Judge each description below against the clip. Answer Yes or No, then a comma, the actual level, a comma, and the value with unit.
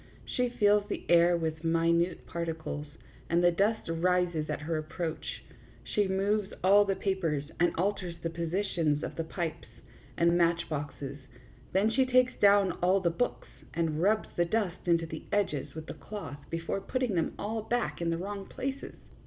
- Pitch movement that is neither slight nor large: Yes, average, 3.6 semitones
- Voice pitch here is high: No, medium, 175 Hz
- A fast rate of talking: No, average, 170 wpm